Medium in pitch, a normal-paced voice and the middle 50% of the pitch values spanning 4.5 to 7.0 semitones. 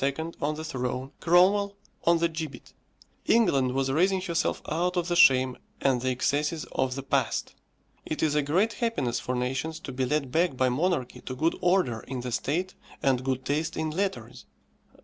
Yes: medium, 150 Hz; average, 180 wpm; average, 4.9 semitones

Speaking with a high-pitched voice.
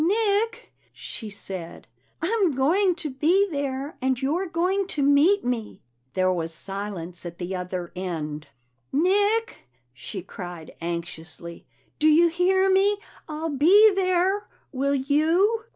Yes: very high, 290 Hz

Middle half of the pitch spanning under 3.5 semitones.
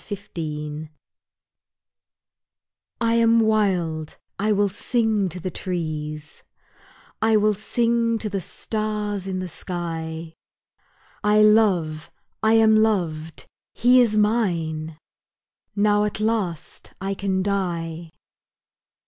No: average, 4.7 semitones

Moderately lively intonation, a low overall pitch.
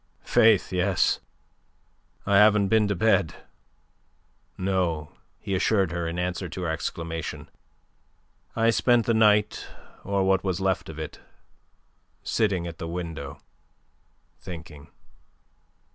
Yes: average, 3.6 semitones; very low, 95 Hz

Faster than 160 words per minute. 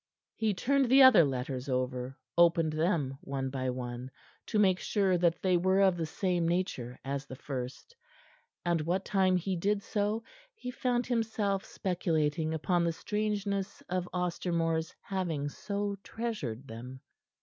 No: average, 150 wpm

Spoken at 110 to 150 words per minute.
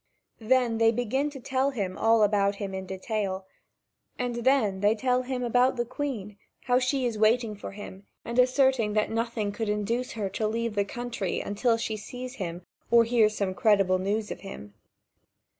No: average, 180 wpm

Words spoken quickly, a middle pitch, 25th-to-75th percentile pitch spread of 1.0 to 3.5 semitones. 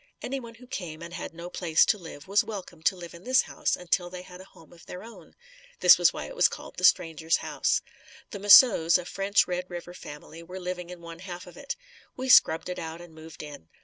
Yes: fast, 235 wpm; medium, 180 Hz; average, 2.8 semitones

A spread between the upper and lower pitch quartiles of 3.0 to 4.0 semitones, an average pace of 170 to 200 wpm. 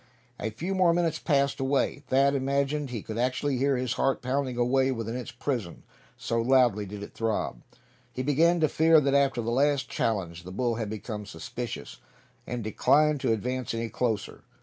Yes: average, 3.6 semitones; average, 180 wpm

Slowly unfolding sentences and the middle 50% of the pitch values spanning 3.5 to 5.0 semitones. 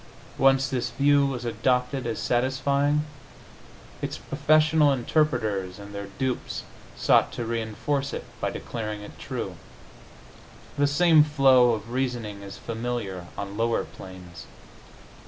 Yes: slow, 120 wpm; average, 4.4 semitones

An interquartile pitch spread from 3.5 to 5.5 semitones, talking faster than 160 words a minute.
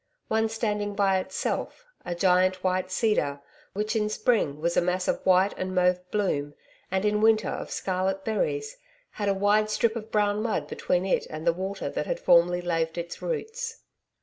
No: average, 3.0 semitones; average, 180 wpm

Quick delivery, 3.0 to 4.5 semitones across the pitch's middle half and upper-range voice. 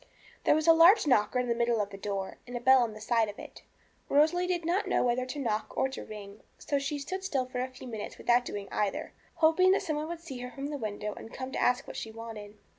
No: fast, 270 wpm; wide, 5.5 semitones; very high, 250 Hz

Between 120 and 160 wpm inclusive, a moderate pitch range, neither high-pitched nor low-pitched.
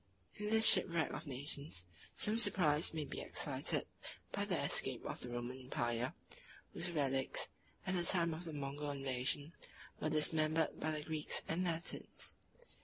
Yes: average, 155 wpm; average, 3.6 semitones; medium, 155 Hz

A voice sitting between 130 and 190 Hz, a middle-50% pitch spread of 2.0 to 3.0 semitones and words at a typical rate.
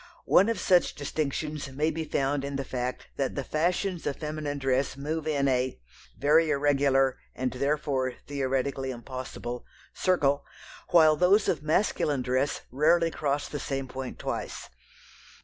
Yes: medium, 140 Hz; narrow, 2.6 semitones; average, 145 wpm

